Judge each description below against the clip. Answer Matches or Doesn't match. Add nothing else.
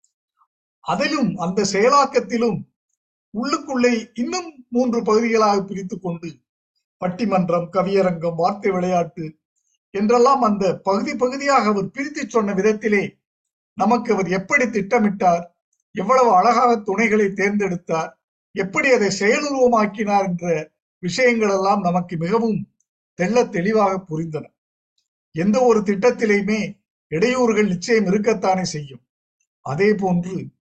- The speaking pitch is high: Matches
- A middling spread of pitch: Matches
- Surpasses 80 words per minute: Matches